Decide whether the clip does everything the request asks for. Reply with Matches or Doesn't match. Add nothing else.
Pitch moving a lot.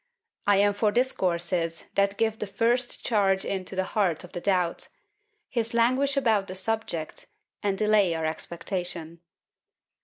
Doesn't match